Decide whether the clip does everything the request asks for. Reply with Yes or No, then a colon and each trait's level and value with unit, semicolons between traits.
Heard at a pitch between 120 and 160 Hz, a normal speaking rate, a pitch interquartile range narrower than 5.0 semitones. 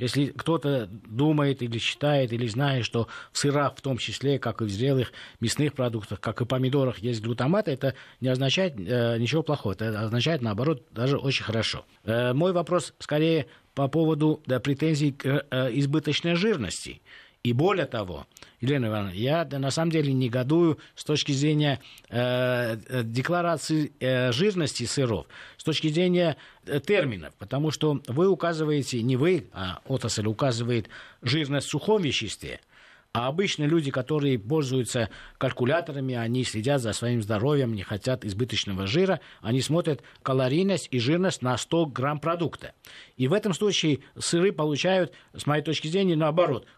Yes: low, 135 Hz; average, 150 wpm; average, 4.4 semitones